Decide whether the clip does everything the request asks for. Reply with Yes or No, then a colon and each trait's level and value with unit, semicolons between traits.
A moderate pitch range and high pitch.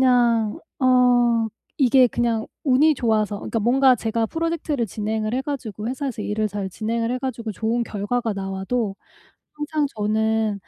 Yes: average, 3.0 semitones; high, 230 Hz